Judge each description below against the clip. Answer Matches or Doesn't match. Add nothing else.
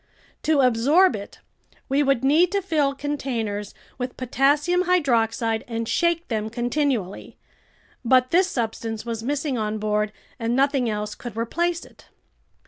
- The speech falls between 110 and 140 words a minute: Matches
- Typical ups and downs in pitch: Matches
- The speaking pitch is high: Matches